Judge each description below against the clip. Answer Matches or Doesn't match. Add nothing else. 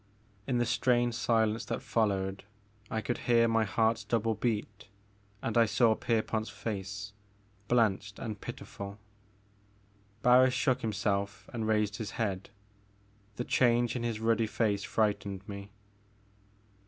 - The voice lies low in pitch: Matches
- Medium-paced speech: Doesn't match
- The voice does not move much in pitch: Matches